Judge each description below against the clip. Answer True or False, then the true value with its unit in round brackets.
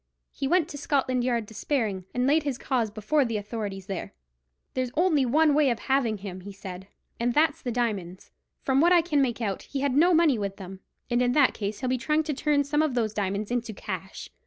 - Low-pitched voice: False (245 Hz)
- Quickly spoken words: True (225 wpm)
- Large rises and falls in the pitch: True (5.7 semitones)